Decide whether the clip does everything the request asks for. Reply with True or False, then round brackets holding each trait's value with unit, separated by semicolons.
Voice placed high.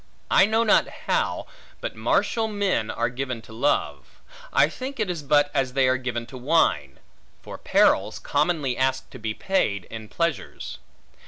False (135 Hz)